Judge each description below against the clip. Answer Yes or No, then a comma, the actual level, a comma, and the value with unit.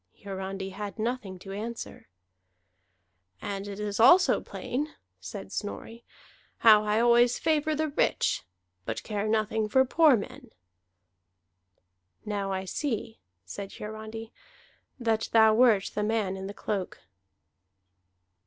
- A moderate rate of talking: No, slow, 120 wpm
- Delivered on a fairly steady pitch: No, average, 3.1 semitones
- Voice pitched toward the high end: Yes, high, 215 Hz